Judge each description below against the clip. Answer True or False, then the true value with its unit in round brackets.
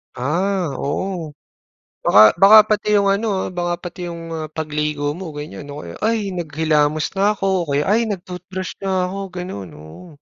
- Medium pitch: True (170 Hz)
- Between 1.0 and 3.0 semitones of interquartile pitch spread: False (4.3 semitones)